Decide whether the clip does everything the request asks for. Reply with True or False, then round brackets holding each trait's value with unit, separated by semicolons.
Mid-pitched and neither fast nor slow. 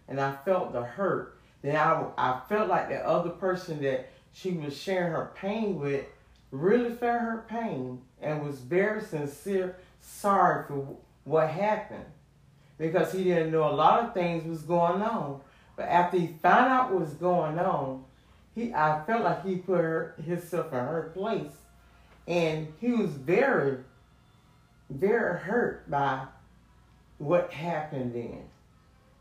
True (165 Hz; 150 wpm)